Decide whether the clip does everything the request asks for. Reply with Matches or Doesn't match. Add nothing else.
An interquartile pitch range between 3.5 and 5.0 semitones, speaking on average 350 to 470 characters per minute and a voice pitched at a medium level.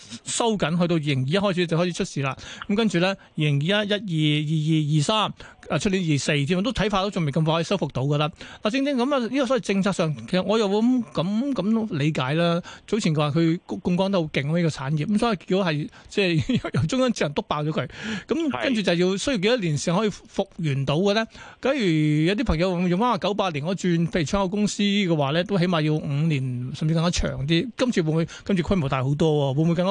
Matches